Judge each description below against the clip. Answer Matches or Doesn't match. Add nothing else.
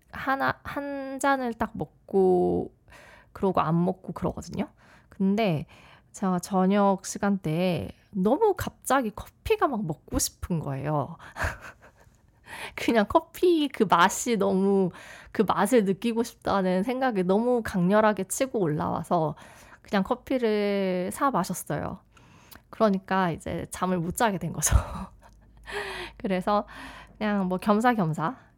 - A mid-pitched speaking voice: Doesn't match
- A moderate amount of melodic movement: Matches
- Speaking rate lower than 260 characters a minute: Matches